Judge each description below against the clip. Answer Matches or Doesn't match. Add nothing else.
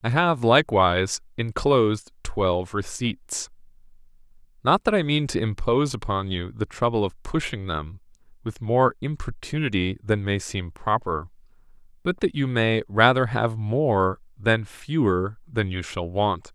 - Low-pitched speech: Matches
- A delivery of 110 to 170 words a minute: Matches